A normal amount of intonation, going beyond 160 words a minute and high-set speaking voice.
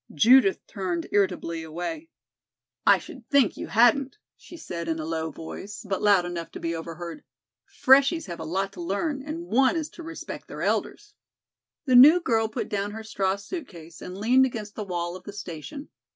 No: wide, 7.4 semitones; average, 190 wpm; high, 205 Hz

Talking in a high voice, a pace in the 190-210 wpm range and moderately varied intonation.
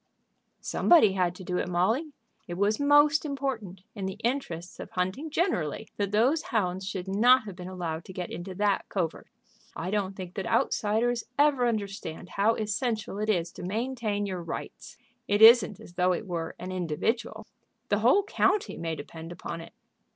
No: high, 200 Hz; average, 175 wpm; average, 4.7 semitones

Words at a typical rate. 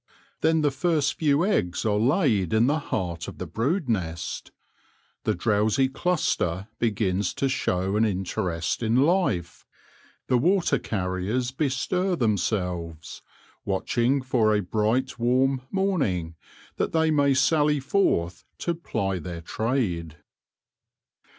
No: slow, 125 wpm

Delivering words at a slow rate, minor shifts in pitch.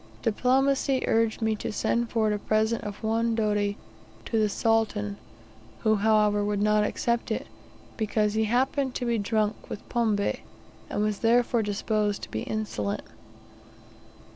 No: average, 145 wpm; narrow, 1.8 semitones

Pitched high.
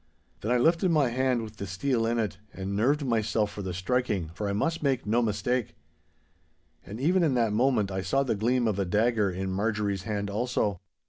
No: low, 110 Hz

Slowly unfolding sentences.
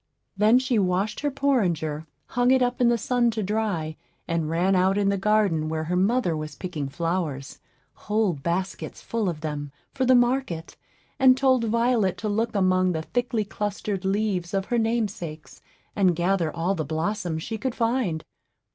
No: average, 175 wpm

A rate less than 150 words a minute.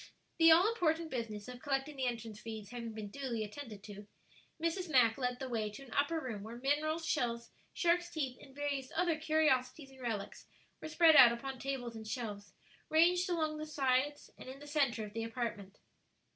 No: average, 190 wpm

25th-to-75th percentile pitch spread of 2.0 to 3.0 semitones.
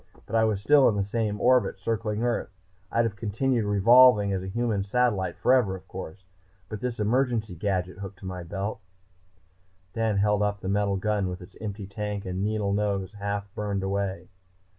Yes: narrow, 2.4 semitones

